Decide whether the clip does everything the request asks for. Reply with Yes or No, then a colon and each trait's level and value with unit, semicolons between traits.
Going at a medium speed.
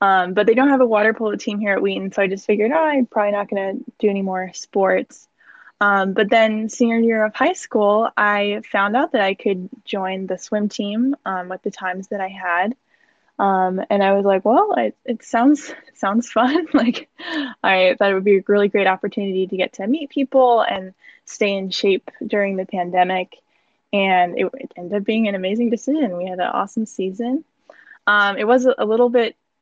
No: fast, 210 wpm